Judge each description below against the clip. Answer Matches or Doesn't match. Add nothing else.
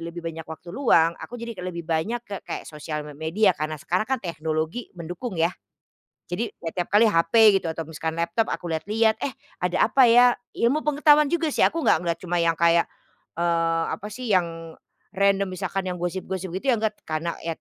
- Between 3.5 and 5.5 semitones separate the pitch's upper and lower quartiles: Matches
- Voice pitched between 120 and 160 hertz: Doesn't match